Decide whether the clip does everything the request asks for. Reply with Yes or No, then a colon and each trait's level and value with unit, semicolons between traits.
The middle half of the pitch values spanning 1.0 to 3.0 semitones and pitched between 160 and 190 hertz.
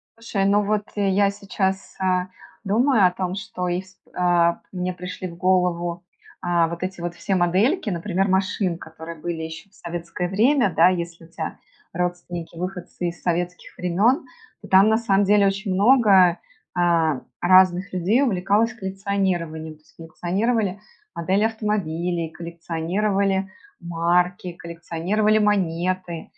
Yes: narrow, 2.6 semitones; medium, 185 Hz